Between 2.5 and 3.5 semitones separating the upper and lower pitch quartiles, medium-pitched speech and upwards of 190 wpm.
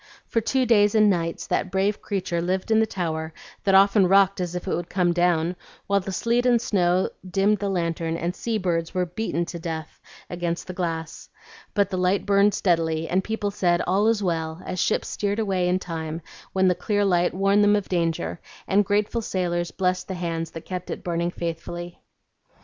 Yes: average, 2.8 semitones; medium, 180 Hz; average, 200 wpm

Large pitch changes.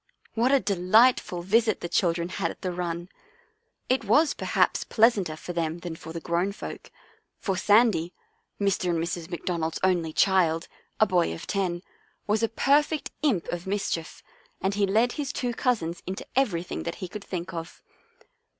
No: average, 4.4 semitones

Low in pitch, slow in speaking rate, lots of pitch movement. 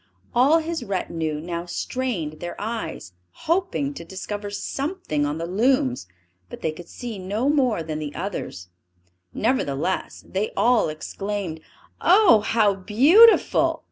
No: high, 205 Hz; slow, 130 wpm; wide, 7.8 semitones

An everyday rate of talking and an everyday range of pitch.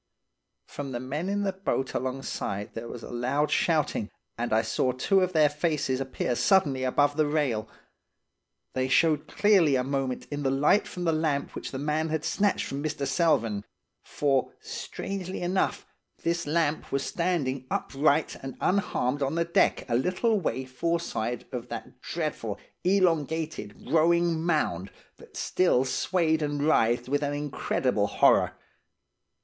Yes: average, 155 wpm; average, 4.4 semitones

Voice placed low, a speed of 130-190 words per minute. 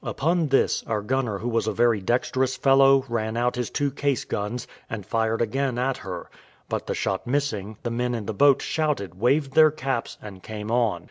No: low, 120 Hz; average, 200 wpm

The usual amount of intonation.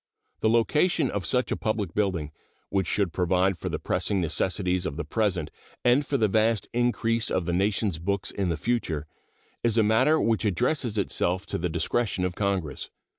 Yes: average, 4.2 semitones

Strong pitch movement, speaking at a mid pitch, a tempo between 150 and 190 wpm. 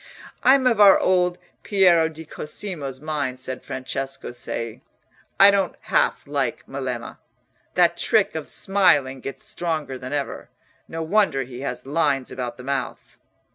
No: wide, 6.1 semitones; medium, 150 Hz; slow, 135 wpm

